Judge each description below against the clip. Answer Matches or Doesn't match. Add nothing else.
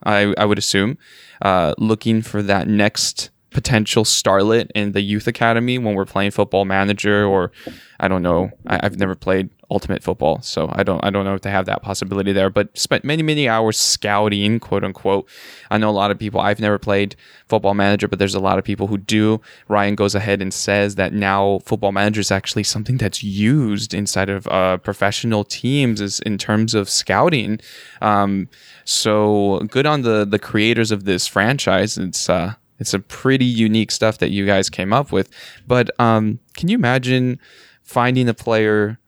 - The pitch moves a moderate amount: Doesn't match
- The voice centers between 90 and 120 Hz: Matches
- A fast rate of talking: Doesn't match